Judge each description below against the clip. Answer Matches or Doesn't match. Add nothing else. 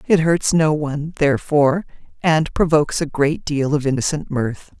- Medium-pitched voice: Matches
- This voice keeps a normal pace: Matches